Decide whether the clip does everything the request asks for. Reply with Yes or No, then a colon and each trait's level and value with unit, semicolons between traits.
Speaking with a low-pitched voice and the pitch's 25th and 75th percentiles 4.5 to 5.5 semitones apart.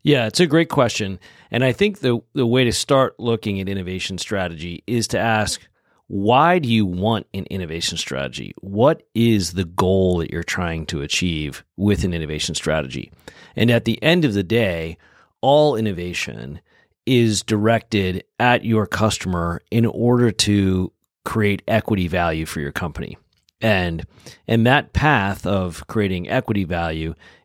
Yes: low, 100 Hz; average, 4.8 semitones